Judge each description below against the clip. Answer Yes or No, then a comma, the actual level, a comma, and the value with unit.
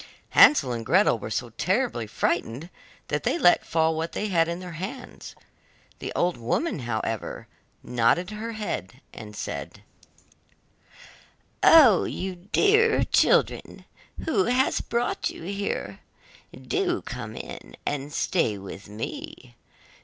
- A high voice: No, medium, 170 Hz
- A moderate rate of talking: No, slow, 125 wpm